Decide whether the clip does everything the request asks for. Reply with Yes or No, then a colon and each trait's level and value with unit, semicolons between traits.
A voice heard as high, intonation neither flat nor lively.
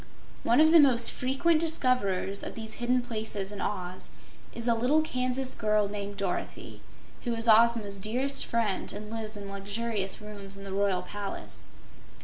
Yes: high, 220 Hz; average, 3.7 semitones